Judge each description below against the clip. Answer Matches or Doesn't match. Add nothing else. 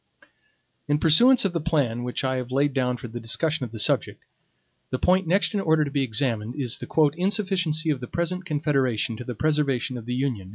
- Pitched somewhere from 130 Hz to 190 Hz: Matches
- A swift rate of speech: Matches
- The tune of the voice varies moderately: Matches